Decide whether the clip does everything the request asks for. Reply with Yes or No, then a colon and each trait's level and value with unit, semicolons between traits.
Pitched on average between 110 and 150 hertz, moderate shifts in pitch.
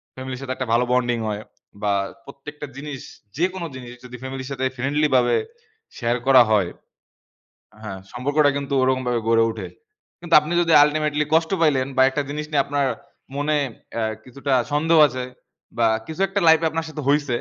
Yes: medium, 140 Hz; average, 3.2 semitones